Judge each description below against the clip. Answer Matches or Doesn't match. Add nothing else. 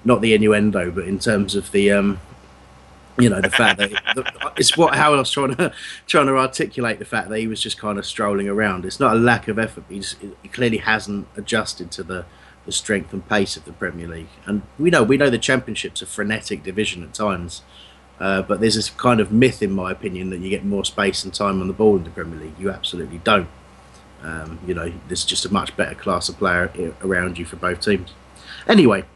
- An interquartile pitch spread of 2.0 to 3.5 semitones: Doesn't match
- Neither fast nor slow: Doesn't match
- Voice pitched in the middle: Doesn't match